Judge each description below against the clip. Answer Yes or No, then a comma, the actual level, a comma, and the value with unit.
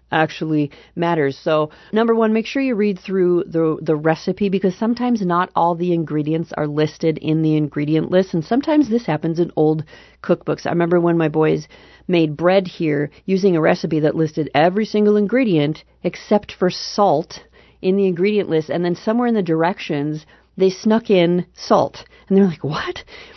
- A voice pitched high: No, medium, 175 Hz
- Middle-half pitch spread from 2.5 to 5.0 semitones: Yes, average, 4.2 semitones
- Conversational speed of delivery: Yes, average, 175 wpm